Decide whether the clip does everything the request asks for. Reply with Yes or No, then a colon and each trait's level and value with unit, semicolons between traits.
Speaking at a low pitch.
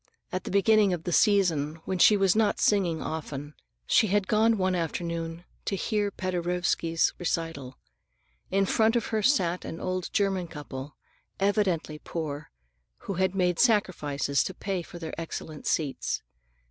No: medium, 180 Hz